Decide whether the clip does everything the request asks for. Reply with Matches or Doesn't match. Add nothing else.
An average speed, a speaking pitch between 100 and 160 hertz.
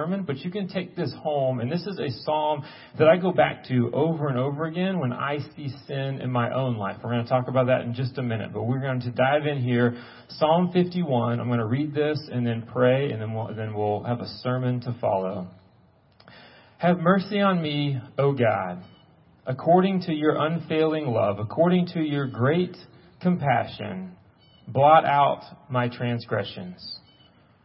Matches